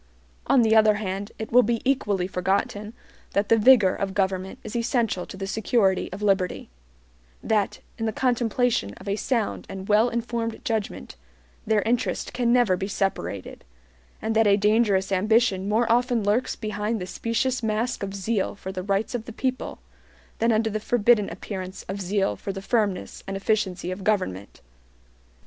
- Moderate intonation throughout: Yes, average, 3.0 semitones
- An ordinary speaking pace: Yes, average, 170 wpm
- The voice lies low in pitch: No, high, 210 Hz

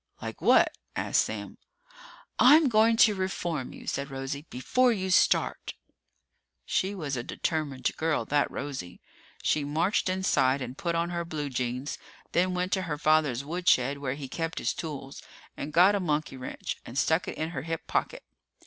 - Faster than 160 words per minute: Yes, average, 170 wpm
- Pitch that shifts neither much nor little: Yes, average, 4.6 semitones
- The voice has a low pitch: No, medium, 155 Hz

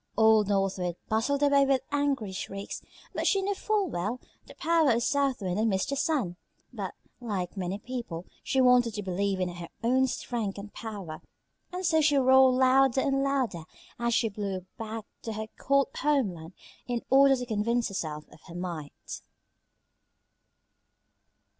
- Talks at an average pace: Yes, average, 160 wpm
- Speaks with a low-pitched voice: No, high, 230 Hz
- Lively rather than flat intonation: Yes, wide, 5.8 semitones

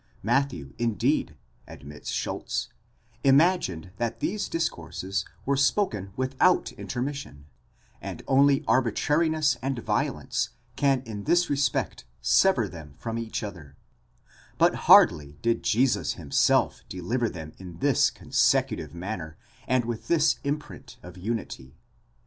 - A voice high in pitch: No, low, 115 Hz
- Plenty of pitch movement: Yes, wide, 7.6 semitones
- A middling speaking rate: No, slow, 115 wpm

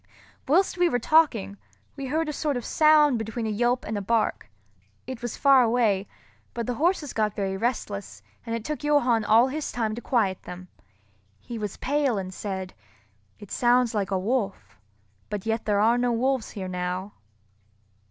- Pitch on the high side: Yes, high, 230 Hz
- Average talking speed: Yes, average, 175 wpm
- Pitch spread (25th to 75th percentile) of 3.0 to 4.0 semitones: No, average, 4.5 semitones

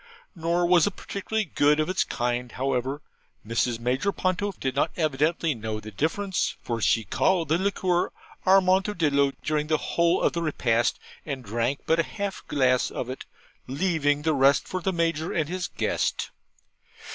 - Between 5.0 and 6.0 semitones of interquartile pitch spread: Yes, wide, 5.5 semitones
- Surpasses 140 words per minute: Yes, average, 165 wpm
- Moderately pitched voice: Yes, medium, 155 Hz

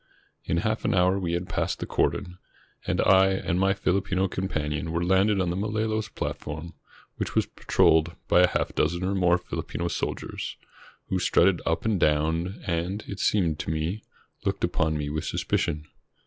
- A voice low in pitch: Yes, very low, 90 Hz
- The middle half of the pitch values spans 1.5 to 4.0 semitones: Yes, average, 2.7 semitones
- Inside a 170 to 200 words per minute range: Yes, average, 175 wpm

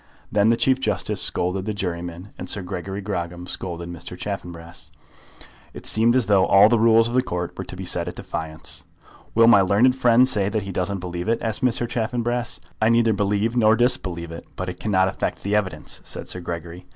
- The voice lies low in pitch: Yes, low, 100 Hz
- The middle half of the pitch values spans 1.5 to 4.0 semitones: No, average, 4.4 semitones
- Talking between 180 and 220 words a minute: Yes, fast, 205 wpm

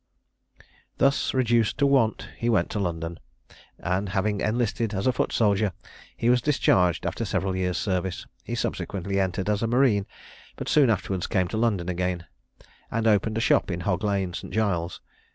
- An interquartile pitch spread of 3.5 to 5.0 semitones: Yes, average, 3.8 semitones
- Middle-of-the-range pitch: No, low, 100 Hz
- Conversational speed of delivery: Yes, average, 170 wpm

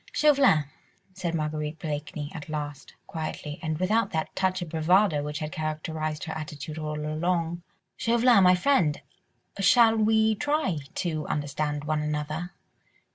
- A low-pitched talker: No, medium, 160 Hz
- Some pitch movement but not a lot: Yes, average, 3.6 semitones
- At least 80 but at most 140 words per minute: Yes, slow, 135 wpm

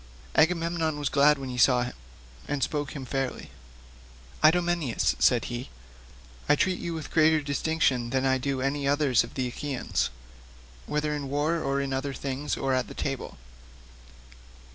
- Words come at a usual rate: Yes, average, 155 wpm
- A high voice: No, medium, 140 Hz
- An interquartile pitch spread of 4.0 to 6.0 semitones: No, narrow, 2.6 semitones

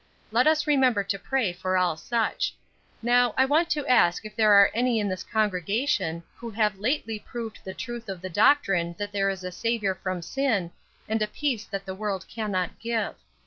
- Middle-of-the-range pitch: No, high, 215 Hz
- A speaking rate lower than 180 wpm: No, average, 195 wpm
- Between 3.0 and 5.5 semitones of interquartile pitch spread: Yes, average, 4.0 semitones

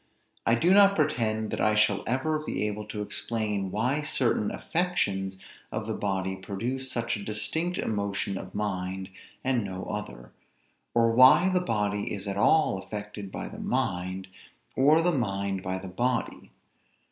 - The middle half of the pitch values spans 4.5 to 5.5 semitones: Yes, average, 4.9 semitones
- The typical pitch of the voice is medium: No, low, 105 Hz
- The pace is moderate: Yes, average, 160 wpm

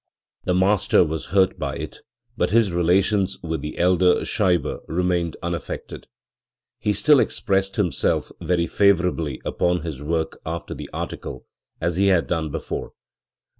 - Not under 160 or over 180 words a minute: No, average, 140 wpm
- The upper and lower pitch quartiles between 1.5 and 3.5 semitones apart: Yes, narrow, 2.5 semitones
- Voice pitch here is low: Yes, very low, 90 Hz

